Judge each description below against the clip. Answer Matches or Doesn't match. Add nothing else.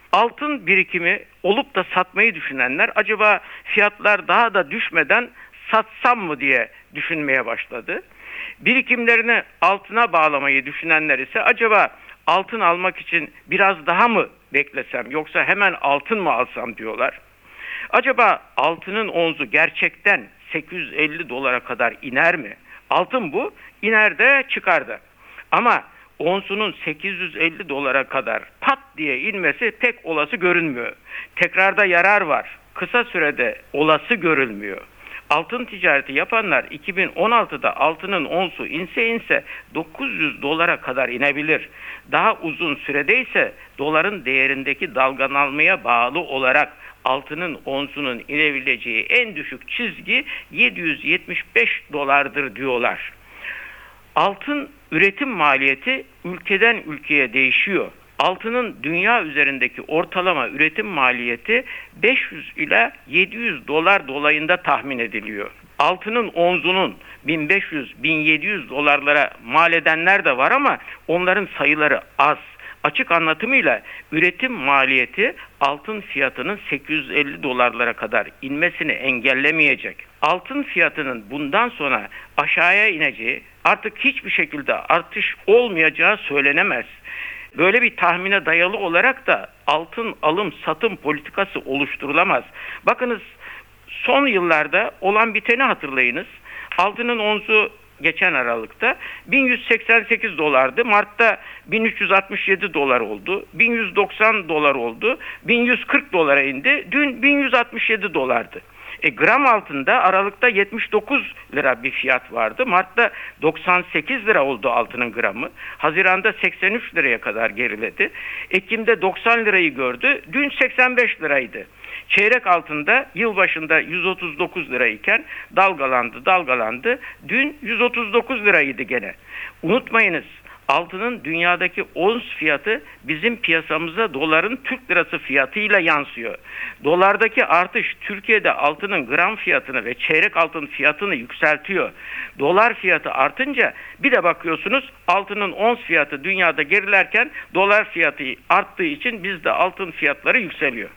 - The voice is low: Doesn't match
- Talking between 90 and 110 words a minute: Matches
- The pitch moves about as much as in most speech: Doesn't match